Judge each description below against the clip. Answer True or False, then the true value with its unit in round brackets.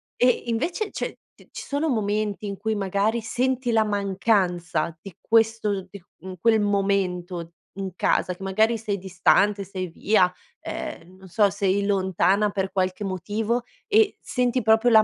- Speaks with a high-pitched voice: True (200 Hz)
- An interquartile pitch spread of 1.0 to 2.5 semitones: False (2.9 semitones)